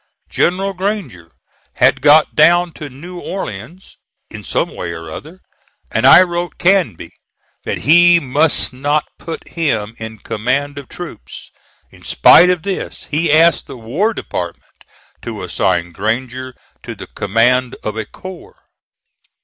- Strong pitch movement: Yes, wide, 7.6 semitones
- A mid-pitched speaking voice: Yes, medium, 145 Hz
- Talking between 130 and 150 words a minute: Yes, average, 140 wpm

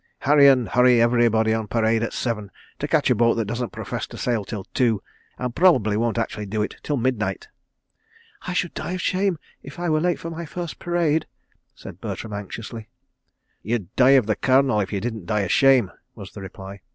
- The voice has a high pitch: No, low, 115 Hz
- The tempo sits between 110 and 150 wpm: No, average, 200 wpm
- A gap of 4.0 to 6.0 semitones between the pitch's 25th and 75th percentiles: Yes, average, 4.5 semitones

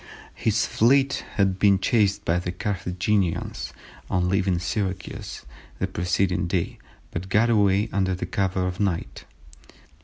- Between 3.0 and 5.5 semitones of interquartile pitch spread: No, narrow, 2.4 semitones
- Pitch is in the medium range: No, very low, 95 Hz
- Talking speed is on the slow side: Yes, slow, 130 wpm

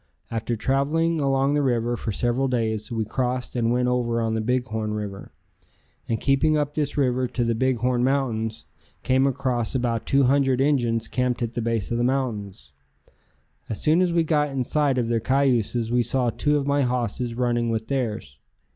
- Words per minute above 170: Yes, average, 190 wpm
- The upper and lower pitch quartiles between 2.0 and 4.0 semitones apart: Yes, average, 2.9 semitones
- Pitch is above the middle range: No, low, 125 Hz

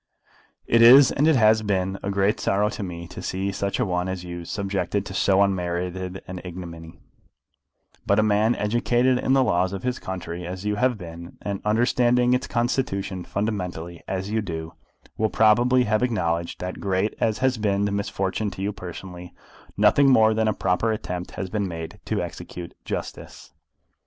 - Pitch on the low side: Yes, low, 100 Hz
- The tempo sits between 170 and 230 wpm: Yes, average, 180 wpm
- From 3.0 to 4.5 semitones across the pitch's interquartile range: Yes, average, 3.5 semitones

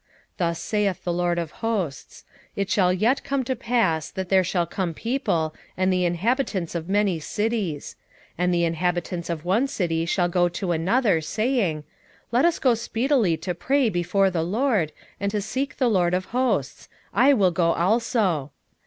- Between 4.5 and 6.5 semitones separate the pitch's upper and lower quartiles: Yes, average, 5.0 semitones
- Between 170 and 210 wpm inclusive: Yes, average, 180 wpm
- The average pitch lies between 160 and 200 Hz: Yes, medium, 185 Hz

